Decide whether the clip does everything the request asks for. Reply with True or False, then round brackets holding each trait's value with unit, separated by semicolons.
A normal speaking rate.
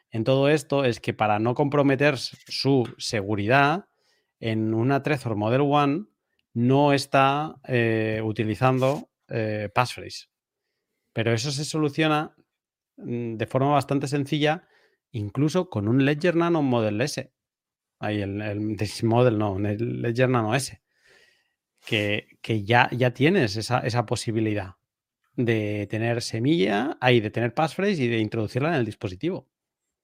True (135 wpm)